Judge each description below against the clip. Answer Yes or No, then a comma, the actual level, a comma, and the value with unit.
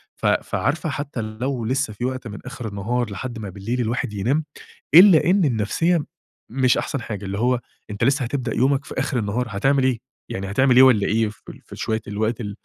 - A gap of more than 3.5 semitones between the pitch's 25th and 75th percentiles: Yes, average, 4.0 semitones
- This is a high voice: No, low, 120 Hz